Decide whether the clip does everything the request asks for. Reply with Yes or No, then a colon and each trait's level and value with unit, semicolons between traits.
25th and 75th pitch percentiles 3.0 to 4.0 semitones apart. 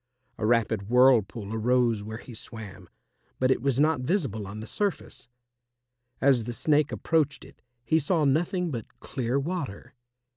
No: average, 4.8 semitones